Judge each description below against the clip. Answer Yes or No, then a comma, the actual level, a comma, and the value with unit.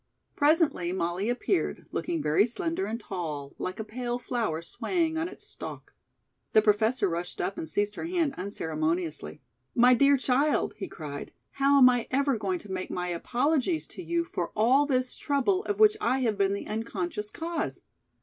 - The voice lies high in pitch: Yes, high, 235 Hz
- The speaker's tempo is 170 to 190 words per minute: Yes, average, 175 wpm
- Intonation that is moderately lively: No, wide, 7.6 semitones